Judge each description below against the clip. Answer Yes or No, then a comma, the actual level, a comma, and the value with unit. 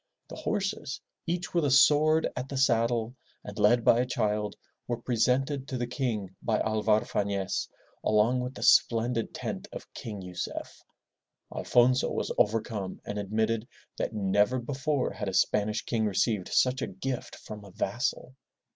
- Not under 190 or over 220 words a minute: No, average, 155 wpm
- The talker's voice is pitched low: Yes, low, 115 Hz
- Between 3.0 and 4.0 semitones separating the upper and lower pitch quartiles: Yes, average, 3.5 semitones